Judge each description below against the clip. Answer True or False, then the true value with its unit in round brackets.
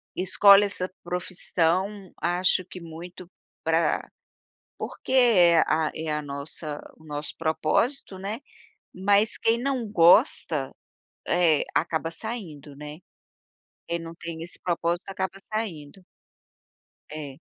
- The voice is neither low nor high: True (175 Hz)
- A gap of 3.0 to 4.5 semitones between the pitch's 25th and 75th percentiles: True (3.7 semitones)